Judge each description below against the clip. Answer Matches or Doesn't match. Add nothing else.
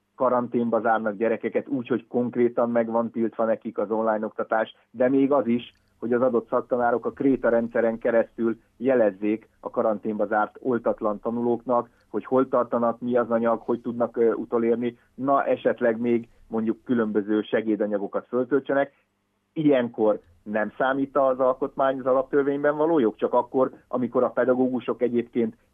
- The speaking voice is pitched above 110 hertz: Matches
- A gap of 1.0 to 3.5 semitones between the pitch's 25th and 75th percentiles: Matches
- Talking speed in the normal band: Matches